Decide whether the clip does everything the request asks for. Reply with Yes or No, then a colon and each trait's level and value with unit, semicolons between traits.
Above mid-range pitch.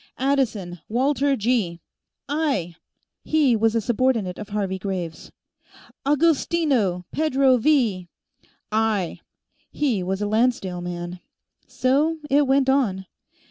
Yes: high, 230 Hz